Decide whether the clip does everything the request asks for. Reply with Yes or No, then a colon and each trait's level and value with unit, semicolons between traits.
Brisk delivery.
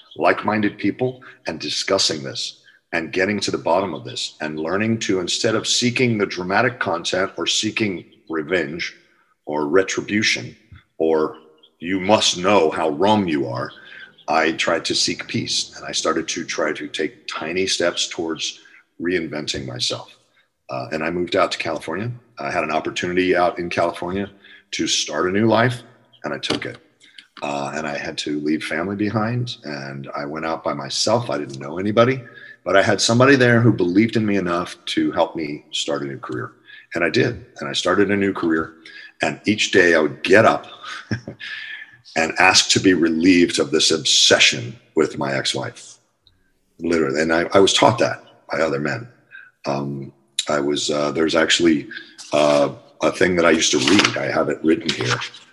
No: average, 180 wpm